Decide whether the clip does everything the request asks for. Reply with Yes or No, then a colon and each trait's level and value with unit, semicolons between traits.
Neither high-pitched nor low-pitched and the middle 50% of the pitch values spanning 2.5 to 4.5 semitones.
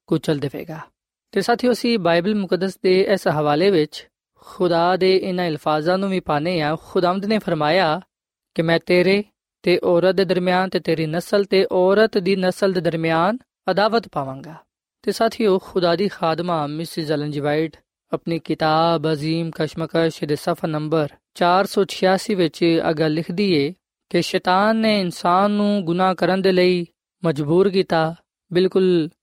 Yes: medium, 180 Hz; average, 2.8 semitones